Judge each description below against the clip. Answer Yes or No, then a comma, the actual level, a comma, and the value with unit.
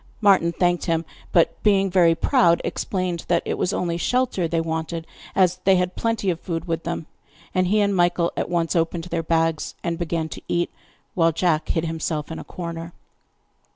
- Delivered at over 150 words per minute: Yes, average, 190 wpm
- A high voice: No, medium, 170 Hz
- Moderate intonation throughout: No, narrow, 1.7 semitones